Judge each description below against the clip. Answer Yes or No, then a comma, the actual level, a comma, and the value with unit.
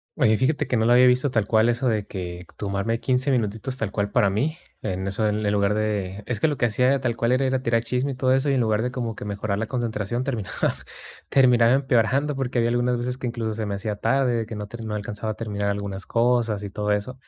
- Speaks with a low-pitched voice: Yes, low, 115 Hz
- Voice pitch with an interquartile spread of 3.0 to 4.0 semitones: Yes, average, 3.4 semitones